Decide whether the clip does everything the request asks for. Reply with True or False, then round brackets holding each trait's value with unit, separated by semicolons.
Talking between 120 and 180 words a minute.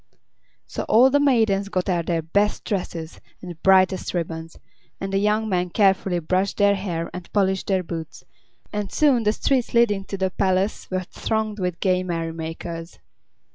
True (170 wpm)